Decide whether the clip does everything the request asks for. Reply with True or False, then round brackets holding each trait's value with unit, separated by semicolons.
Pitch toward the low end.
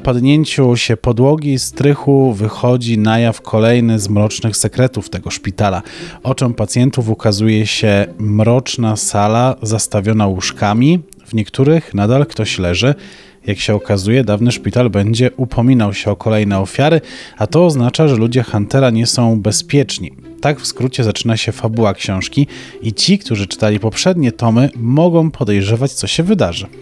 True (115 Hz)